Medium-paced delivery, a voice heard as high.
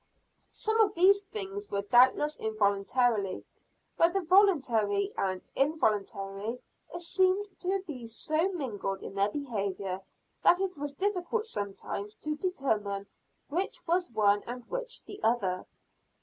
No: slow, 125 wpm; very high, 260 Hz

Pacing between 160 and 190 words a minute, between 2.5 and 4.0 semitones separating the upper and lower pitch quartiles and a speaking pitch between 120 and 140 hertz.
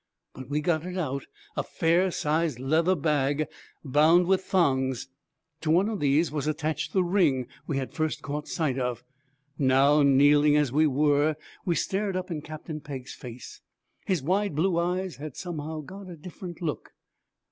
No: average, 170 wpm; average, 3.6 semitones; medium, 155 Hz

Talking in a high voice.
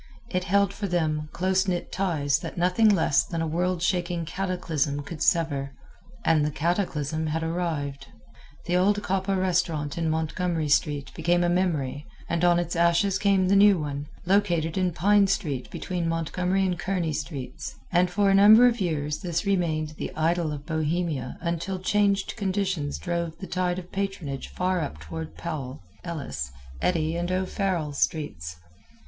No: medium, 170 Hz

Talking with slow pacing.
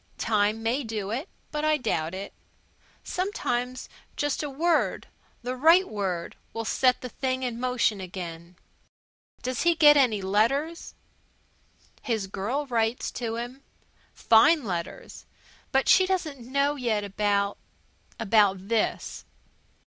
Yes: slow, 125 wpm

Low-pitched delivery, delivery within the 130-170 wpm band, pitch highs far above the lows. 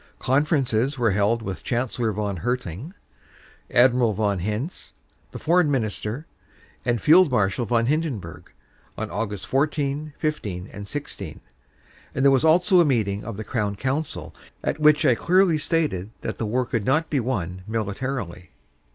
Yes: low, 125 Hz; average, 150 wpm; wide, 6.1 semitones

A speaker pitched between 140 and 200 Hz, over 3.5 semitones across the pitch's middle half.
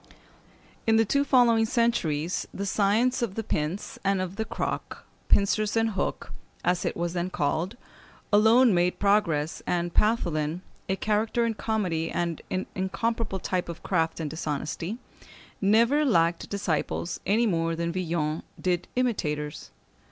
Yes: high, 190 Hz; average, 4.8 semitones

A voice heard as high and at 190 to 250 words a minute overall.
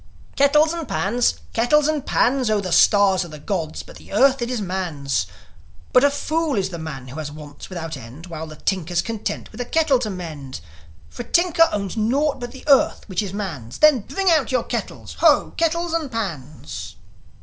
Yes: high, 210 Hz; average, 200 wpm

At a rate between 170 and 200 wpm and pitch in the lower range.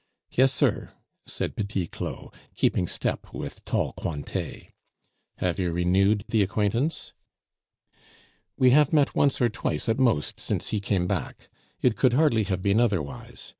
No: average, 145 wpm; low, 105 Hz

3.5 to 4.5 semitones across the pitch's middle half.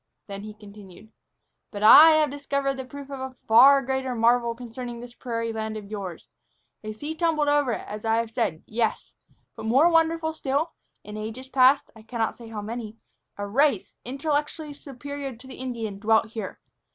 Yes: average, 4.2 semitones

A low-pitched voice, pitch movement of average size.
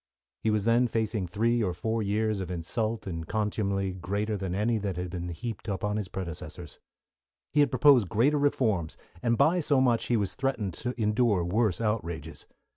Yes: low, 105 Hz; average, 3.6 semitones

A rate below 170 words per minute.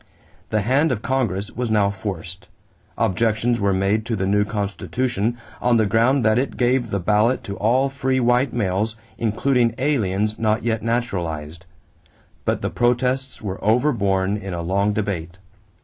Yes: average, 155 wpm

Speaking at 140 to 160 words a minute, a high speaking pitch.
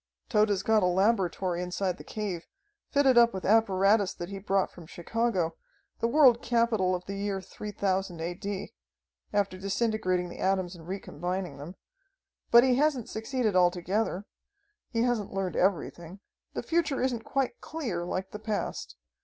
Yes: average, 155 wpm; high, 195 Hz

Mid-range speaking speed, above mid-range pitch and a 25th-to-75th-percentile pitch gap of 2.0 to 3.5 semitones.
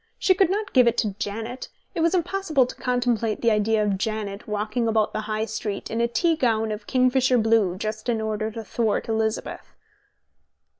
Yes: average, 190 wpm; high, 225 Hz; average, 2.7 semitones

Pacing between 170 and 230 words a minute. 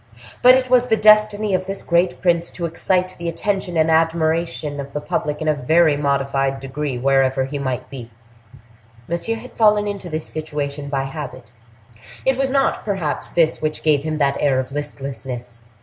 Yes: average, 180 wpm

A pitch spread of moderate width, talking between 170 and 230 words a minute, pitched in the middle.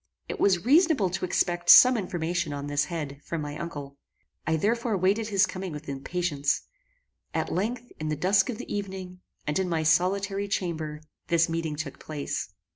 Yes: average, 4.3 semitones; average, 175 wpm; medium, 175 Hz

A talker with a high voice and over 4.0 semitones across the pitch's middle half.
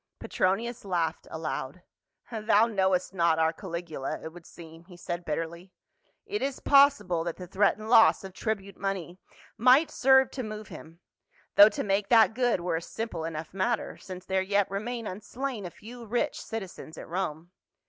Yes: high, 195 Hz; average, 4.7 semitones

